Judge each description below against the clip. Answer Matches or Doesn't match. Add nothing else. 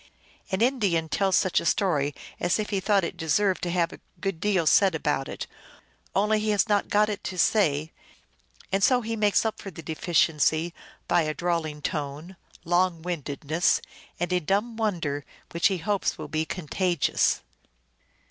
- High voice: Doesn't match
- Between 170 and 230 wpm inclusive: Matches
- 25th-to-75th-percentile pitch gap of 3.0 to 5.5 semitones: Matches